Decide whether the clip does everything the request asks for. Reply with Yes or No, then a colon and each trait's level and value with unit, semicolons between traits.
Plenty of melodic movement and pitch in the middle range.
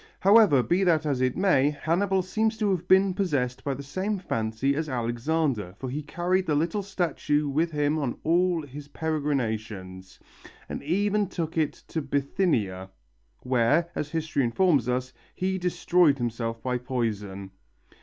Yes: wide, 6.2 semitones; medium, 150 Hz